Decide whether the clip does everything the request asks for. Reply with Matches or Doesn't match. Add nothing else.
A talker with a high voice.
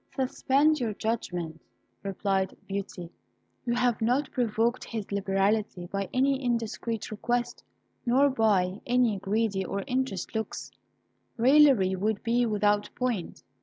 Matches